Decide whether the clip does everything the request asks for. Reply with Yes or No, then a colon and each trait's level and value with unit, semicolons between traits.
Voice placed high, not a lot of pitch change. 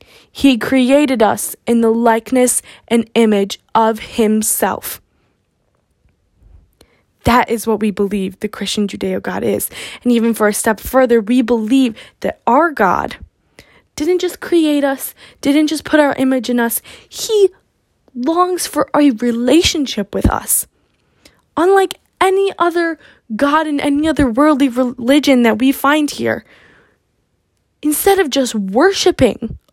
No: very high, 260 Hz; average, 4.9 semitones